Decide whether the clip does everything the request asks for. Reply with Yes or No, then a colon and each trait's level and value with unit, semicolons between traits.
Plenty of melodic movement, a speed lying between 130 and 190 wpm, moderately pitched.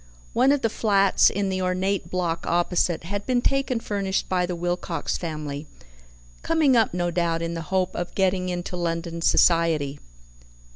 No: average, 2.9 semitones; average, 160 wpm; medium, 180 Hz